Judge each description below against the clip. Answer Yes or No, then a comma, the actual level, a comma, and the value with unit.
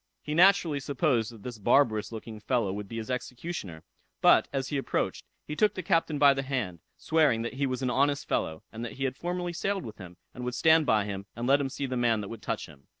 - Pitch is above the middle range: No, low, 130 Hz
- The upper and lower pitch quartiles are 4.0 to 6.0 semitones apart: Yes, average, 4.9 semitones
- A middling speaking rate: No, fast, 245 wpm